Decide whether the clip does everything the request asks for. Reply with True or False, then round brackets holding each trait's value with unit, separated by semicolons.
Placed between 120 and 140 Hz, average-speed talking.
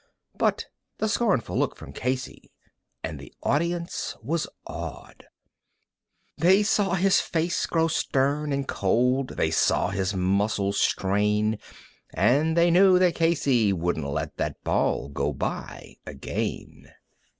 False (135 Hz; 125 wpm)